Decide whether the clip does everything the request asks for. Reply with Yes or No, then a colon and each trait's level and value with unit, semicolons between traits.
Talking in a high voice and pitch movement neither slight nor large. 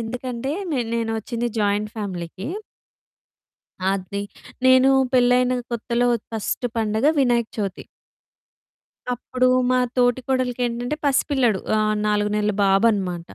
Yes: high, 230 Hz; average, 3.2 semitones